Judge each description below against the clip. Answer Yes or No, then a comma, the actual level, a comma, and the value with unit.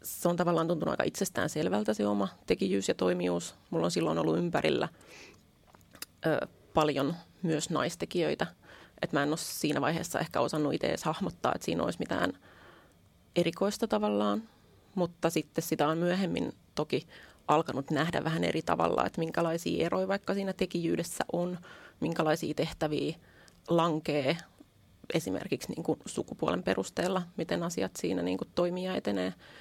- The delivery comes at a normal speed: Yes, average, 140 wpm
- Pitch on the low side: No, medium, 155 Hz